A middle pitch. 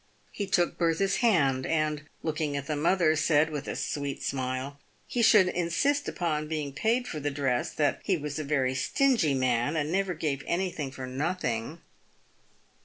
Yes: medium, 155 Hz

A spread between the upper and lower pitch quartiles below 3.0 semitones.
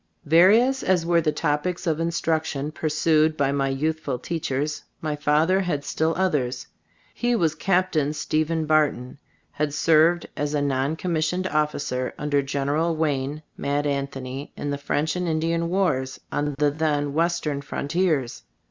Yes: narrow, 2.6 semitones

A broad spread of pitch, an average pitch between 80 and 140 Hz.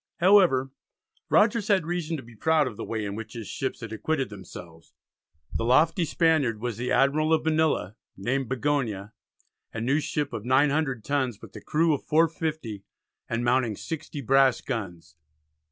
Yes: wide, 5.8 semitones; low, 135 Hz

